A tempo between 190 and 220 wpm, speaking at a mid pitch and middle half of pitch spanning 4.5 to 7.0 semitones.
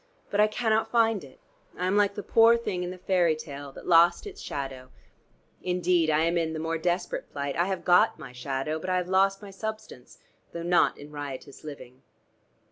Yes: fast, 205 wpm; medium, 175 Hz; average, 4.8 semitones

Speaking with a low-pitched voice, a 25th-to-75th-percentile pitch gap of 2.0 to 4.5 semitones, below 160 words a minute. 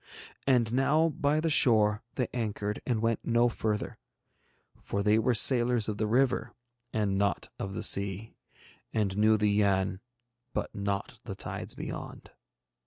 Yes: low, 110 Hz; average, 3.0 semitones; average, 150 wpm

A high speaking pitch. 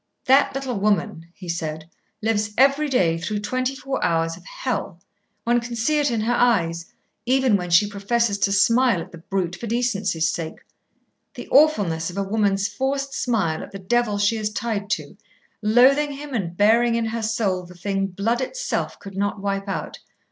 Yes: high, 210 Hz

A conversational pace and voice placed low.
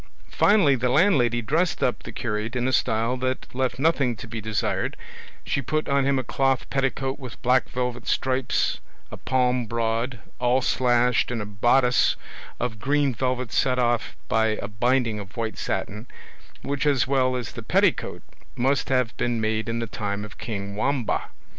Yes: average, 170 wpm; low, 125 Hz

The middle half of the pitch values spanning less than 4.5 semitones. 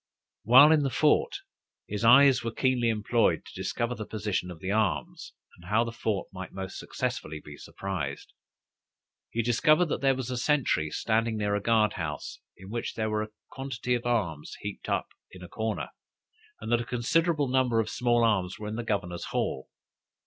Yes: average, 4.0 semitones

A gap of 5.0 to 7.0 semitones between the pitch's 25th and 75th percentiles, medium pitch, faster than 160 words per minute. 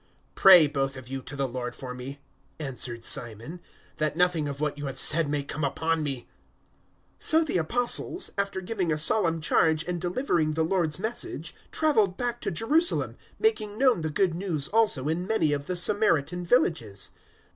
Yes: average, 5.3 semitones; medium, 160 Hz; average, 180 wpm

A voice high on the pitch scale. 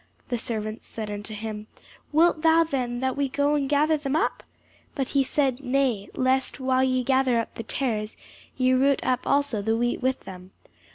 Yes: very high, 260 Hz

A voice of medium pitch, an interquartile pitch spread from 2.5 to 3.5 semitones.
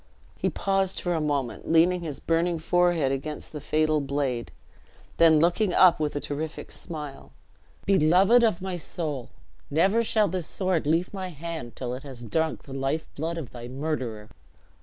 No: medium, 160 Hz; average, 3.9 semitones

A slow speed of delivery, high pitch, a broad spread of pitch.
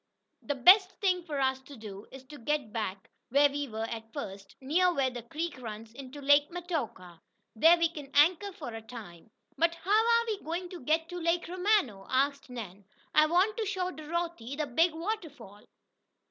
No: average, 190 wpm; very high, 290 Hz; wide, 6.7 semitones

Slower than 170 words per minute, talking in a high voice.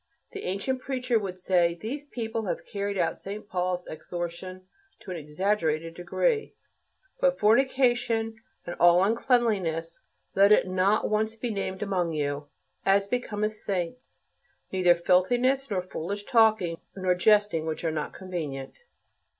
Yes: slow, 135 wpm; high, 195 Hz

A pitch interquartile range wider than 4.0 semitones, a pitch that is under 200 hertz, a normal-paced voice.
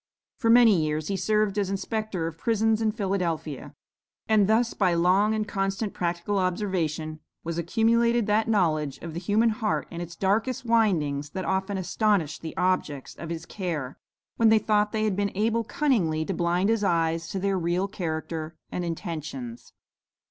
Yes: average, 4.5 semitones; high, 190 Hz; average, 170 wpm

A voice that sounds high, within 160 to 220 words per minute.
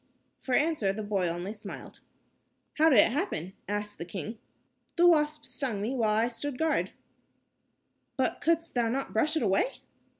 Yes: high, 240 Hz; average, 165 wpm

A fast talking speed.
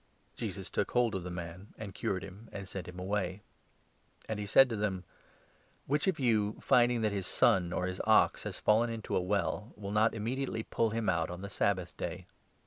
Yes: fast, 210 wpm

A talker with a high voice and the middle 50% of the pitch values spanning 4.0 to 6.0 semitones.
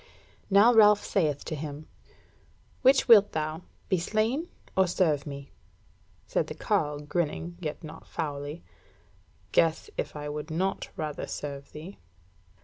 No: medium, 160 Hz; average, 4.6 semitones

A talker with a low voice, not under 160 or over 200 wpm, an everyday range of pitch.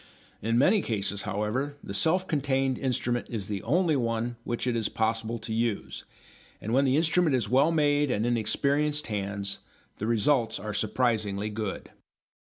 Yes: low, 120 Hz; average, 165 wpm; average, 4.7 semitones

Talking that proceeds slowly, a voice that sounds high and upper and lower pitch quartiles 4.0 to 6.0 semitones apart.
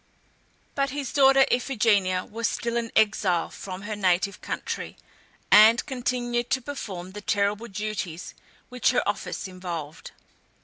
Yes: slow, 130 wpm; high, 215 Hz; average, 4.4 semitones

